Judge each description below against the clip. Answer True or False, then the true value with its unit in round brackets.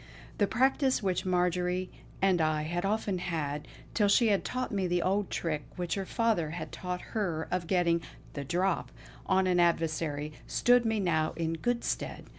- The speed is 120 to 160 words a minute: False (175 wpm)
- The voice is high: False (180 Hz)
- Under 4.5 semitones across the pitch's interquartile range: True (3.3 semitones)